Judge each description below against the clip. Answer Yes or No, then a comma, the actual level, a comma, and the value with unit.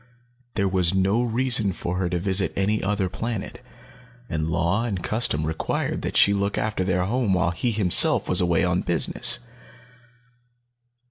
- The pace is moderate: Yes, average, 155 wpm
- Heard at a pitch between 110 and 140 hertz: No, very low, 95 Hz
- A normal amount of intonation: Yes, average, 3.2 semitones